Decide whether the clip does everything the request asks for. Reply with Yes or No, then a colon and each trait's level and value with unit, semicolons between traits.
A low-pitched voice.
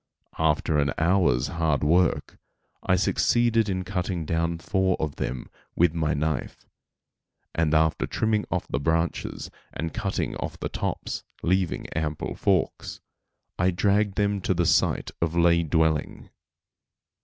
Yes: very low, 85 Hz